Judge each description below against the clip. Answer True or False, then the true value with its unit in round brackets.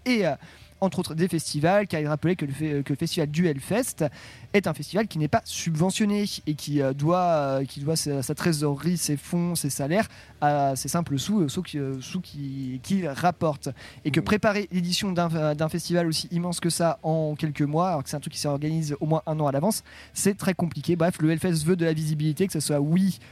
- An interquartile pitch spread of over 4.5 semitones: False (3.3 semitones)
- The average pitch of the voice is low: False (160 Hz)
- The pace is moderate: False (230 wpm)